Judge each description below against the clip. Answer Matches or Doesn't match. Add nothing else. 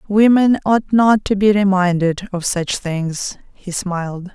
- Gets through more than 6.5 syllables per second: Doesn't match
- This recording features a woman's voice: Matches